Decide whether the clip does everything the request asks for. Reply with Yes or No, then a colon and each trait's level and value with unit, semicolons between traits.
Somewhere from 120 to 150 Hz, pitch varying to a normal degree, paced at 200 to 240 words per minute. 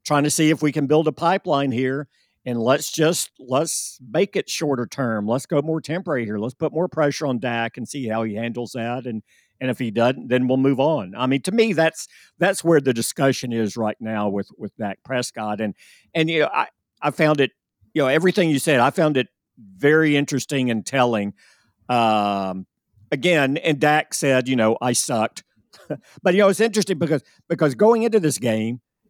Yes: low, 135 Hz; average, 5.0 semitones; fast, 205 wpm